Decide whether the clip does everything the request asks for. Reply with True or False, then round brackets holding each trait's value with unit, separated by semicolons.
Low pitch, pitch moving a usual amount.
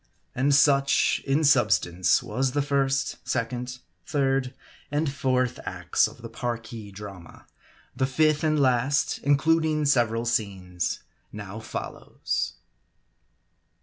True (130 Hz; 3.9 semitones)